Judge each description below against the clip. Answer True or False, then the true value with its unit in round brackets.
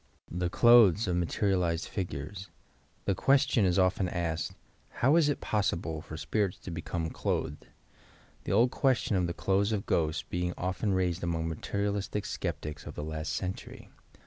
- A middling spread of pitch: True (3.5 semitones)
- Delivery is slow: False (175 wpm)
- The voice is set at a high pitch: False (90 Hz)